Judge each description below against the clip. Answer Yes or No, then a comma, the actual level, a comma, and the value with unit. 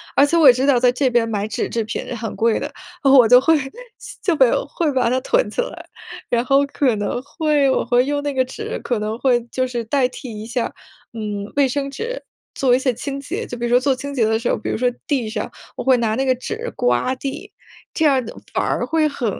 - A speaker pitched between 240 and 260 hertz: Yes, very high, 255 Hz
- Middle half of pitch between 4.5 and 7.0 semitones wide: No, average, 3.1 semitones